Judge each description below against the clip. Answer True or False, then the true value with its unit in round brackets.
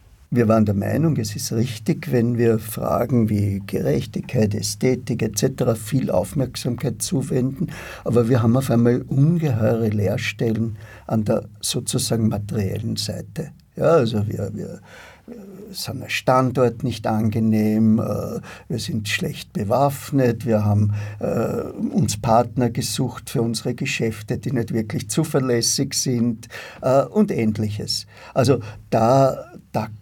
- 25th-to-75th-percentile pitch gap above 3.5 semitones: False (3.0 semitones)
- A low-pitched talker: True (115 Hz)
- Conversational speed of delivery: False (120 wpm)